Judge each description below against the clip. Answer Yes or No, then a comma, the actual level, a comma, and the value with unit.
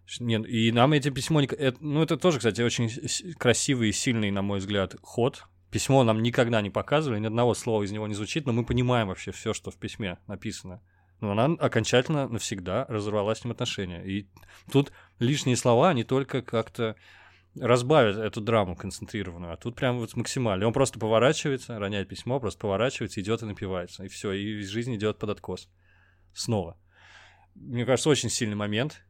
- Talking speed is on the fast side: Yes, fast, 175 wpm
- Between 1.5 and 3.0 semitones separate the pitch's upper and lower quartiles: No, average, 3.9 semitones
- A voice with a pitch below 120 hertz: Yes, low, 110 Hz